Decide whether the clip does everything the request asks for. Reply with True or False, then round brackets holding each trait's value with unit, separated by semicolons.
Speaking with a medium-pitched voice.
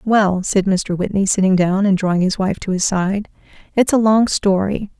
False (195 Hz)